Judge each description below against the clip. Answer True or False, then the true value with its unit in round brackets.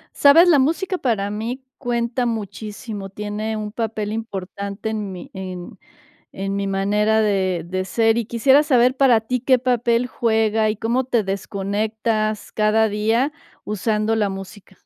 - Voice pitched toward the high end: True (220 Hz)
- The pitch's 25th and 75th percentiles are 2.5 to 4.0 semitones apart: True (2.8 semitones)